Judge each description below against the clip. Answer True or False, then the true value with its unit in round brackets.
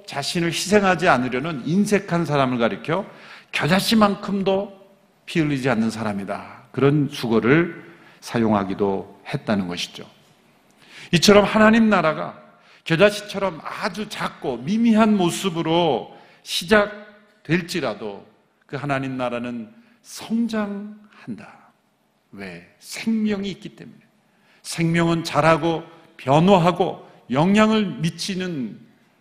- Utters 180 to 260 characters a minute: True (245 characters per minute)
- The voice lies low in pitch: False (180 Hz)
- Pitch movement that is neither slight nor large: False (6.1 semitones)